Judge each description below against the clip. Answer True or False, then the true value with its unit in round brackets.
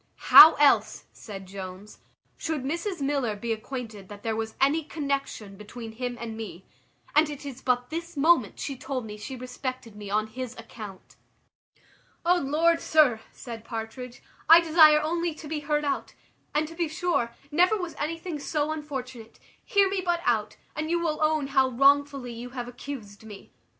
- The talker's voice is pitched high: True (270 Hz)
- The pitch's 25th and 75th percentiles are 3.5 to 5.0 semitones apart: False (5.5 semitones)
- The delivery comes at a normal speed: True (170 wpm)